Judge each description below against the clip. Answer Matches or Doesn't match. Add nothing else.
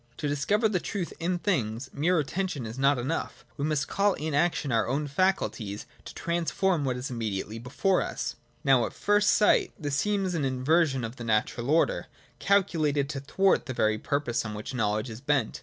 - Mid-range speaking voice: Matches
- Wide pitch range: Matches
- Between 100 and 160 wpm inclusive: Doesn't match